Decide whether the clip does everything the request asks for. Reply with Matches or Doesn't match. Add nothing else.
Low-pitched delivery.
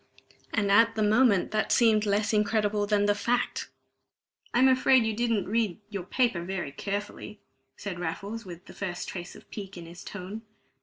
Doesn't match